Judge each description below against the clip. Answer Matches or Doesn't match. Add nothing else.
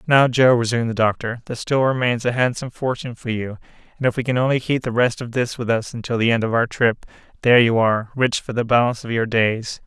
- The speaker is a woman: Doesn't match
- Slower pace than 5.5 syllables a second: Doesn't match